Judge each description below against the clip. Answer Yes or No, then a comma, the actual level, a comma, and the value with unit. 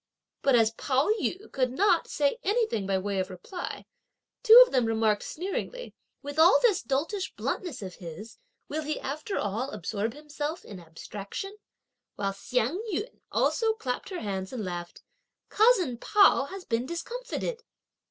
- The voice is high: Yes, very high, 275 Hz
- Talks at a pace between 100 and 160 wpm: Yes, average, 150 wpm